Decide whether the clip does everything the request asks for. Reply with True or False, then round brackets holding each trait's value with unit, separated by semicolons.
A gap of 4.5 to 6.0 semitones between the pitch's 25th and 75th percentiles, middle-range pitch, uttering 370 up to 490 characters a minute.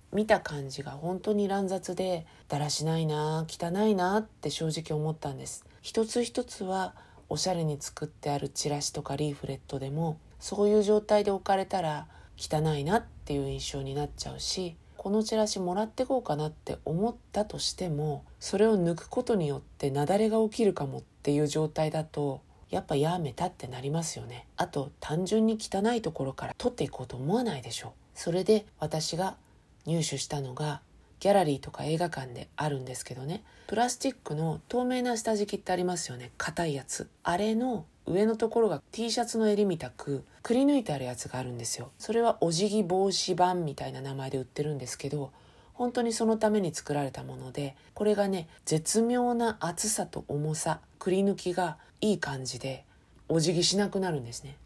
False (6.5 semitones; 165 Hz; 380 characters per minute)